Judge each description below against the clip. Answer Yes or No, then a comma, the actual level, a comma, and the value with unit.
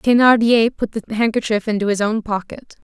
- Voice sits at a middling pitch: No, high, 220 Hz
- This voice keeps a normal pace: Yes, average, 165 wpm